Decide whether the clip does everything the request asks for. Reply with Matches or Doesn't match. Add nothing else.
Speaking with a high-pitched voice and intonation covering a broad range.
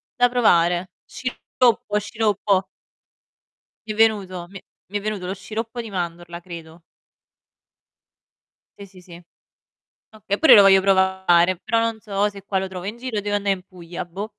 Doesn't match